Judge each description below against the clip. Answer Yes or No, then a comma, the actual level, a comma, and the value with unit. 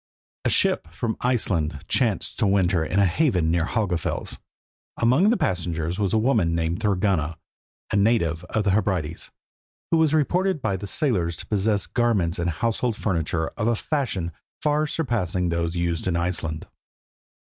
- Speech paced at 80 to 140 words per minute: No, average, 160 wpm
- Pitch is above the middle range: No, very low, 95 Hz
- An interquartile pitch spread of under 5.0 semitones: No, wide, 5.5 semitones